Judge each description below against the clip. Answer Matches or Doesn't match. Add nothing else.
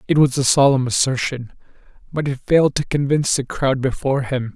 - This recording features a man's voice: Matches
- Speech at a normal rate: Matches